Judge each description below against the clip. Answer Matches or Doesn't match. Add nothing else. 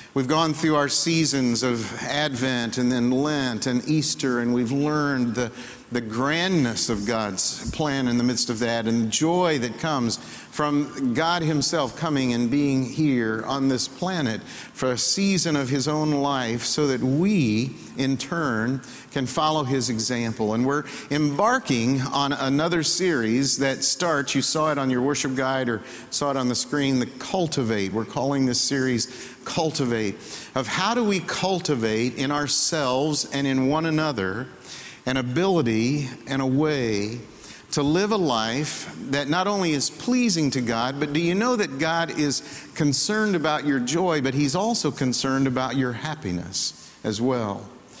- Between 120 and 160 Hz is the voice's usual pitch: Matches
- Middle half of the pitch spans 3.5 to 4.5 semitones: Matches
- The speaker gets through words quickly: Doesn't match